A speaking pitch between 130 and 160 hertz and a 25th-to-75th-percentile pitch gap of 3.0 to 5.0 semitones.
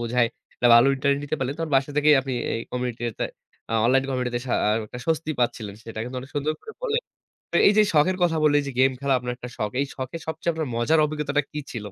Yes: low, 135 Hz; average, 3.8 semitones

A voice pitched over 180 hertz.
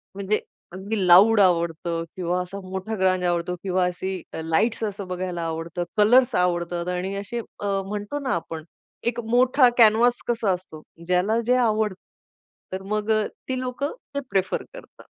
Yes: high, 190 Hz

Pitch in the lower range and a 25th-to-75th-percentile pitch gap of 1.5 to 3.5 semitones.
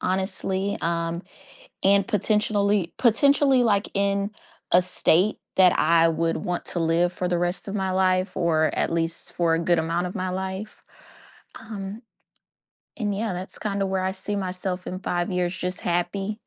No: medium, 185 Hz; narrow, 2.4 semitones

